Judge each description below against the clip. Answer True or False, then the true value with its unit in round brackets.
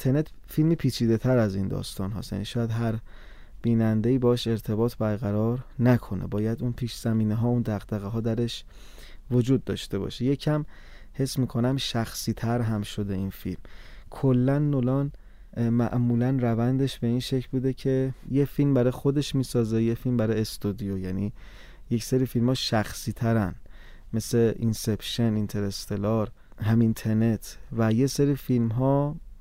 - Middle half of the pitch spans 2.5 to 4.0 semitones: True (3.1 semitones)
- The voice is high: False (115 Hz)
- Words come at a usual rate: True (145 wpm)